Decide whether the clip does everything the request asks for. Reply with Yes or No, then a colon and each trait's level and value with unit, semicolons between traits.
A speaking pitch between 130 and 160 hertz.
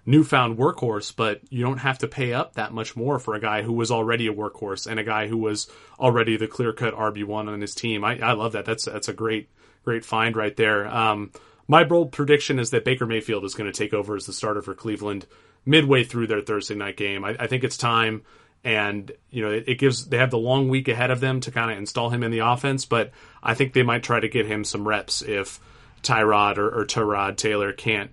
No: low, 115 Hz